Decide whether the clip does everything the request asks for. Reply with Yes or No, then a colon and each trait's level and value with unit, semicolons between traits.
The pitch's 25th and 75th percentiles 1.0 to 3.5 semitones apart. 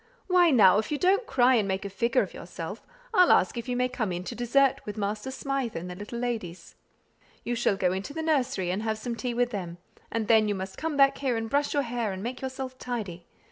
No: average, 4.7 semitones